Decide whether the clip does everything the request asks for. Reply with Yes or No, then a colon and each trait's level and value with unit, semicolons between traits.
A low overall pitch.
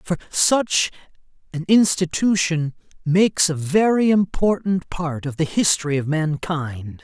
No: medium, 170 Hz